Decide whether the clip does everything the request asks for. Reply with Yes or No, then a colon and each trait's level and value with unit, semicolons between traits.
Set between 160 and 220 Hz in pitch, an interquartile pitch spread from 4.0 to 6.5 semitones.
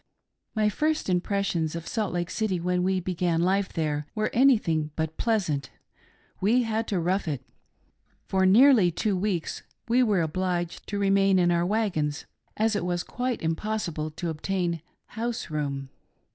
Yes: medium, 185 Hz; average, 4.4 semitones